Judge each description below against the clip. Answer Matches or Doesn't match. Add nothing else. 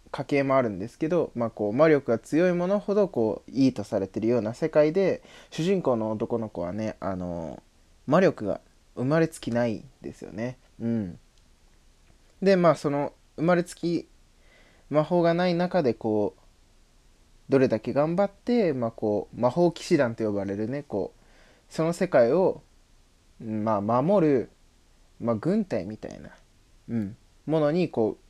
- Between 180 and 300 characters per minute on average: Matches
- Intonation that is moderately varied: Doesn't match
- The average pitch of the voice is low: Matches